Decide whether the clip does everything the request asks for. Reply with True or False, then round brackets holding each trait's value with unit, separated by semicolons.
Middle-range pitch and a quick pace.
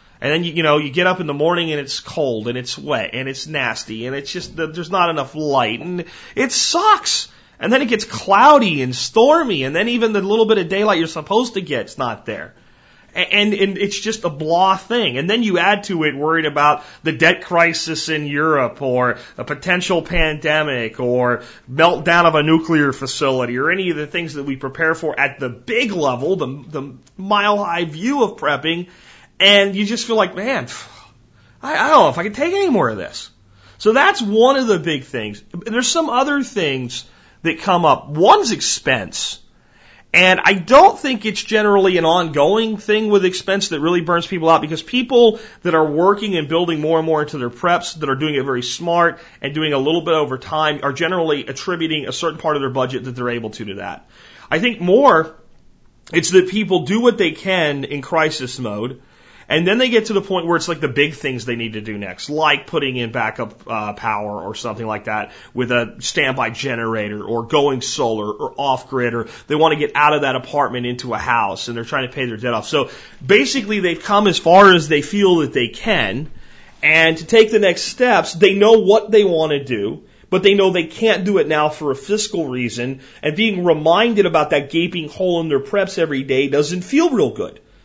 True (160 Hz; 215 wpm)